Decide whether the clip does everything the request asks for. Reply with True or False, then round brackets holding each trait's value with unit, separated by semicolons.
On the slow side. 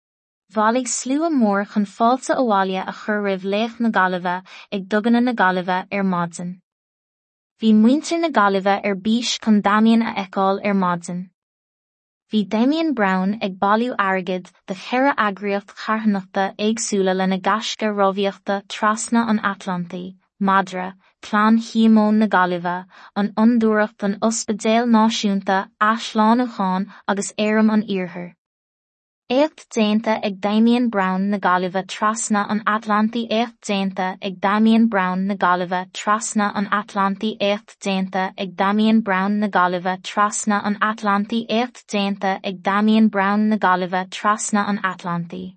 True (125 wpm)